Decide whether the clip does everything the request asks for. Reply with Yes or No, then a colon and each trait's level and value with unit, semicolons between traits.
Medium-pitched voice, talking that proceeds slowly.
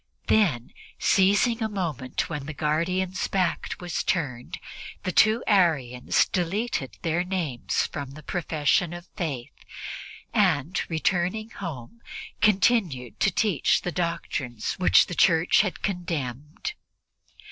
Yes: medium, 175 Hz; slow, 115 wpm